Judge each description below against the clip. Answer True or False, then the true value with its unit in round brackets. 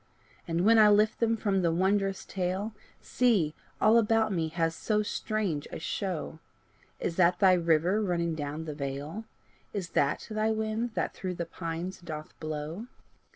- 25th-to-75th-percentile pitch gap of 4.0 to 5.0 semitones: True (4.7 semitones)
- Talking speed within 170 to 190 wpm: False (160 wpm)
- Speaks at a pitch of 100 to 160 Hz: False (185 Hz)